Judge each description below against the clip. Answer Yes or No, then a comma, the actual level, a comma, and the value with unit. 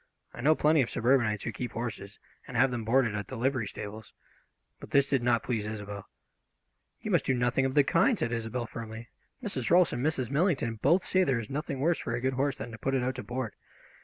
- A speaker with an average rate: No, fast, 230 wpm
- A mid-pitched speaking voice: No, low, 125 Hz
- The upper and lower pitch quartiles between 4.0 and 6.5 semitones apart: No, average, 3.2 semitones